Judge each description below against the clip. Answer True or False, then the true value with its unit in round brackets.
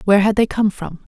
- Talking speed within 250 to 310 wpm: True (260 wpm)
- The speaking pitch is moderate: False (205 Hz)